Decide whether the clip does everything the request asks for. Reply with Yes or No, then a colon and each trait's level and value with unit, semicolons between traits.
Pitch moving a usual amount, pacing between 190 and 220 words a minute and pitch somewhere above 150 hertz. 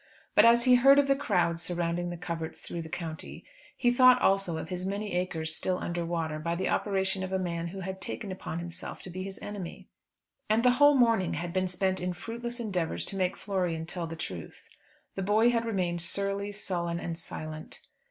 Yes: average, 3.4 semitones; fast, 205 wpm; medium, 185 Hz